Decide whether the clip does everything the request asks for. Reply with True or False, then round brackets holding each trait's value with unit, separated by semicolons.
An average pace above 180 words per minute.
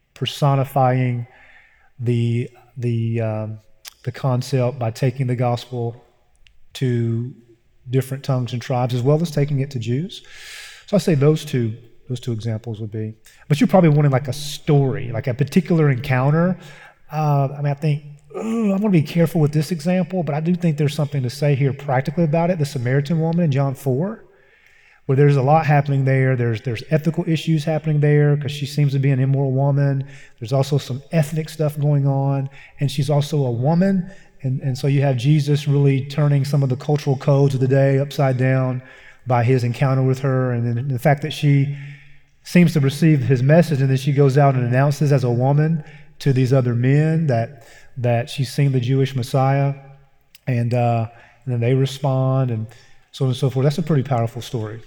True (195 wpm)